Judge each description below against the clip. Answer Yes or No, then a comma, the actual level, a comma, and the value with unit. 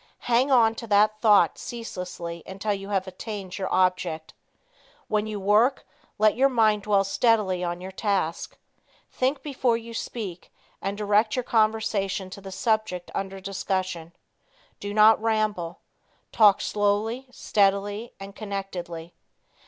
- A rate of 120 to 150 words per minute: Yes, slow, 135 wpm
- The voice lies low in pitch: No, high, 205 Hz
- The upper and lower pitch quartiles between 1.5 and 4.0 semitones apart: Yes, average, 2.7 semitones